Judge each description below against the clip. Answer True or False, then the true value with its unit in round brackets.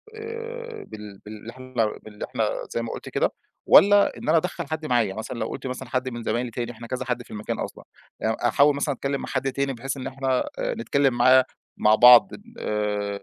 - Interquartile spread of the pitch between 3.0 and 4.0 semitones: True (3.5 semitones)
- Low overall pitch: True (130 Hz)